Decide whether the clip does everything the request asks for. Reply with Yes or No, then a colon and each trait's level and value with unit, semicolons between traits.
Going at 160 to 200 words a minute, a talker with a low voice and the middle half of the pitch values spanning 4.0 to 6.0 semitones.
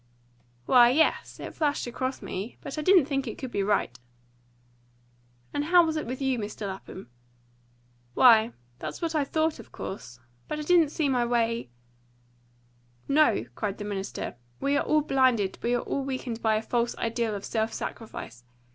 No: average, 175 wpm; high, 240 Hz; wide, 5.6 semitones